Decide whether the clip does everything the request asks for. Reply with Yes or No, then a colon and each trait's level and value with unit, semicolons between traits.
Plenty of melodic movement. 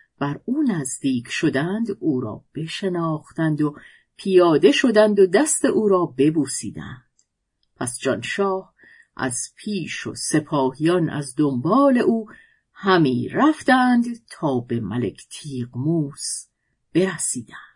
Yes: wide, 7.1 semitones